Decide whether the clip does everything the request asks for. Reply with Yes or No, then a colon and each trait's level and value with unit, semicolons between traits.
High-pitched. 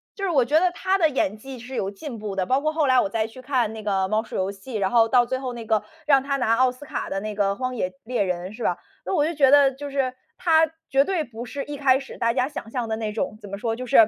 Yes: very high, 250 Hz